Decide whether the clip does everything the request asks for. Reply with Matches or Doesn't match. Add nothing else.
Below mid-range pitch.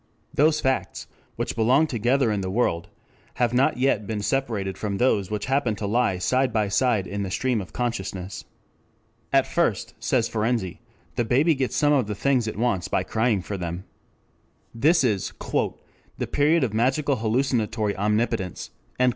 Matches